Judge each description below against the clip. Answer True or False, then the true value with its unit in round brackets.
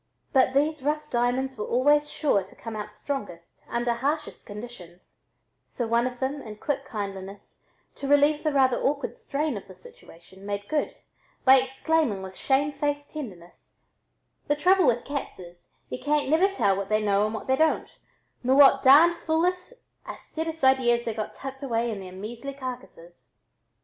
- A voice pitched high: True (260 Hz)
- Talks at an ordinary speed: True (170 wpm)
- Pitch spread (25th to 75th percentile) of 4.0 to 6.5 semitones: True (5.6 semitones)